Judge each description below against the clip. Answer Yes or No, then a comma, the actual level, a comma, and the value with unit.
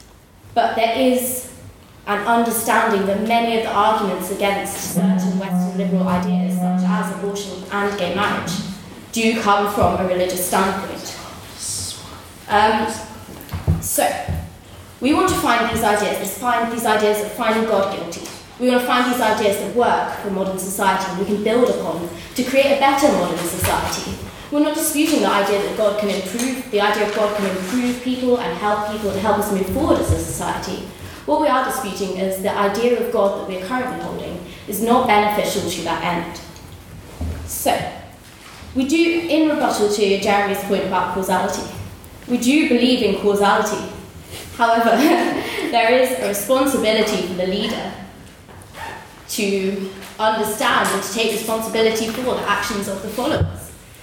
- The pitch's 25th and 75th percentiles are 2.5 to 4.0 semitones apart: Yes, average, 3.7 semitones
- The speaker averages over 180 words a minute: No, average, 160 wpm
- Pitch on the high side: Yes, high, 205 Hz